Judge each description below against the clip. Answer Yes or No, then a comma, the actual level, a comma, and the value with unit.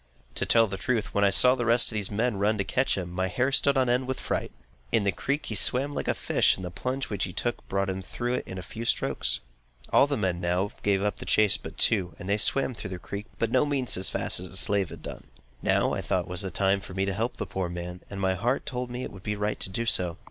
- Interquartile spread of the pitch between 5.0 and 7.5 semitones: No, average, 4.5 semitones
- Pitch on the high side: No, low, 105 Hz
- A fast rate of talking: Yes, fast, 290 wpm